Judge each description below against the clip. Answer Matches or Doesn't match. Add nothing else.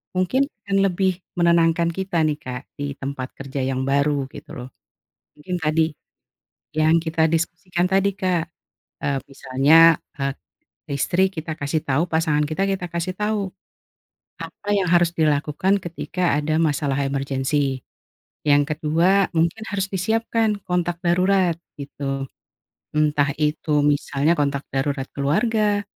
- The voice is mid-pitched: Matches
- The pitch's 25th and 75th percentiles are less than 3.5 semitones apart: Doesn't match